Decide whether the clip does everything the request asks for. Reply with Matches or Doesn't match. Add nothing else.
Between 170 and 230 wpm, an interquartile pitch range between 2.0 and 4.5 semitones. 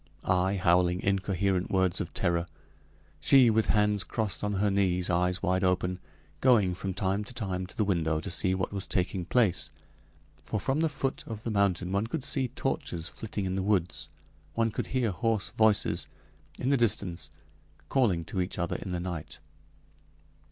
Matches